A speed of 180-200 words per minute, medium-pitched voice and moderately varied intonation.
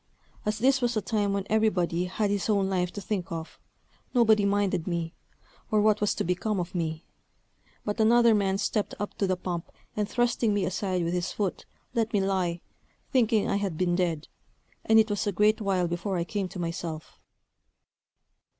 No: average, 185 wpm; high, 200 Hz; average, 3.2 semitones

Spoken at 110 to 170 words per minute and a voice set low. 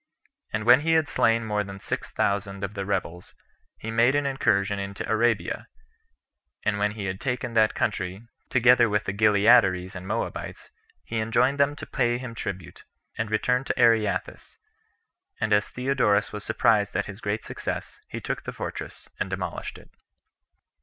Yes: average, 165 wpm; low, 110 Hz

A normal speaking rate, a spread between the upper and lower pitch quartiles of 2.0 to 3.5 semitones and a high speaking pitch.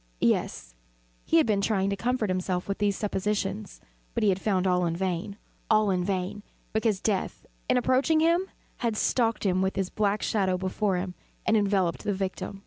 Yes: average, 180 wpm; narrow, 2.5 semitones; high, 200 Hz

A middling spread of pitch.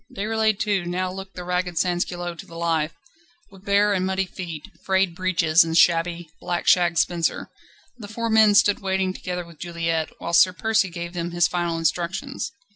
No: narrow, 2.2 semitones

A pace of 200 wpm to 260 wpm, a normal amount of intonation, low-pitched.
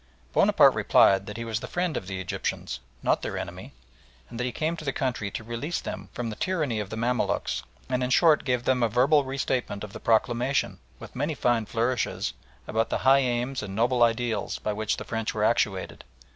Yes: fast, 205 wpm; average, 3.2 semitones; low, 120 Hz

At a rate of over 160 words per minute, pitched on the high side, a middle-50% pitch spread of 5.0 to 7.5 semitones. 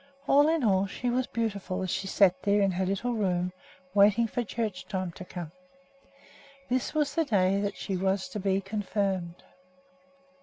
No: average, 175 wpm; high, 200 Hz; average, 3.5 semitones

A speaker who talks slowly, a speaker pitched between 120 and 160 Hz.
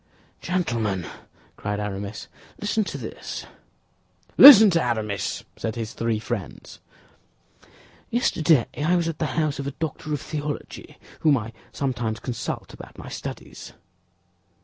Yes: slow, 125 wpm; low, 135 Hz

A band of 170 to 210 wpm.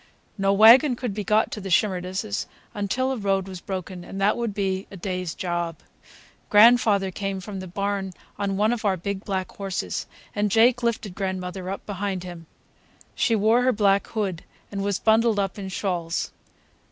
Yes: average, 175 wpm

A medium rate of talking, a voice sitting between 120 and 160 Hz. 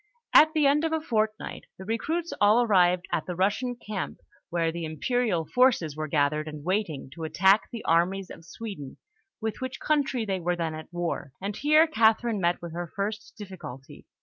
No: average, 185 wpm; high, 195 Hz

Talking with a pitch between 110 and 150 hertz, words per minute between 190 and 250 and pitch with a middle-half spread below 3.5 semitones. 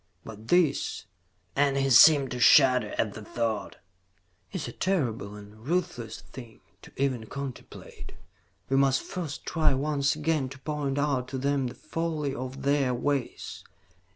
No: low, 135 Hz; average, 155 wpm; average, 3.0 semitones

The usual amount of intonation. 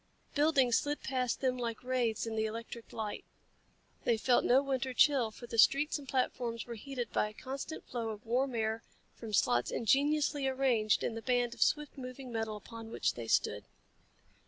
Yes: average, 3.0 semitones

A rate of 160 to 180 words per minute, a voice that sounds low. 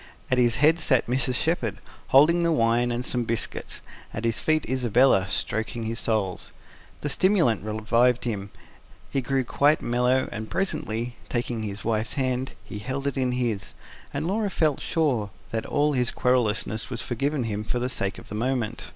Yes: average, 175 wpm; low, 125 Hz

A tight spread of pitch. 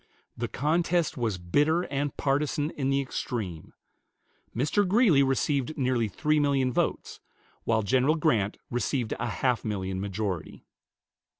No: average, 5.2 semitones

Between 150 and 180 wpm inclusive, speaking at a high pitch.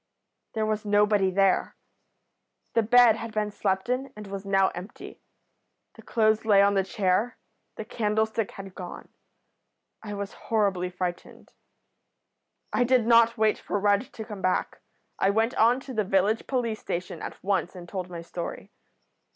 Yes: average, 160 wpm; high, 210 Hz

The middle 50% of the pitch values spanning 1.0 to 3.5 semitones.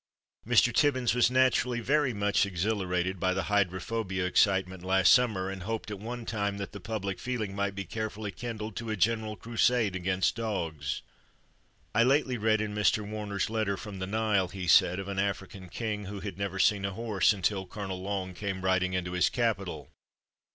Yes: average, 2.8 semitones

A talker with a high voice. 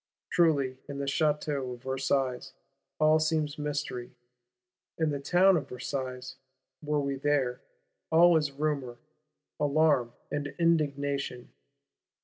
No: medium, 140 Hz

